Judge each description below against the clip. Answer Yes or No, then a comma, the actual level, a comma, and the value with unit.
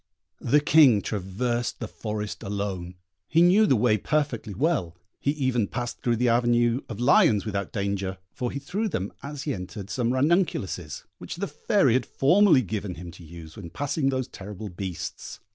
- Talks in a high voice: No, low, 120 Hz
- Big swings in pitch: Yes, wide, 6.0 semitones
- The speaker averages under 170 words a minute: No, average, 175 wpm